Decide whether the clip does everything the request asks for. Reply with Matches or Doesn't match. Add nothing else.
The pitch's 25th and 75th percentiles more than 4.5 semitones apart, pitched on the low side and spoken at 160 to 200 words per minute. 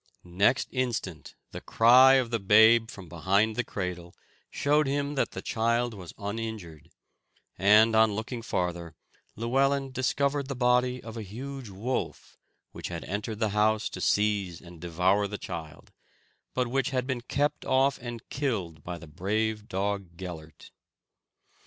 Doesn't match